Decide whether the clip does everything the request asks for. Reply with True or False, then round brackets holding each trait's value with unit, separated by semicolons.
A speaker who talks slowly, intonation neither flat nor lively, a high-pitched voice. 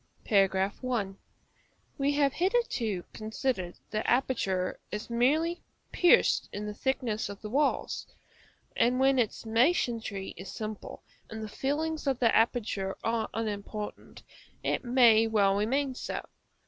True (130 wpm; 4.2 semitones; 225 Hz)